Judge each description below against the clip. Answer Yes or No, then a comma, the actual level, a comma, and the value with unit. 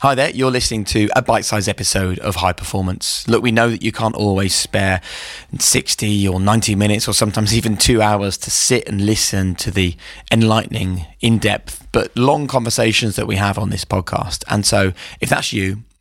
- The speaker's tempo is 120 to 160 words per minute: No, average, 195 wpm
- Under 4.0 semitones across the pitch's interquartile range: Yes, narrow, 2.6 semitones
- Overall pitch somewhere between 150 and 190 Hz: No, low, 105 Hz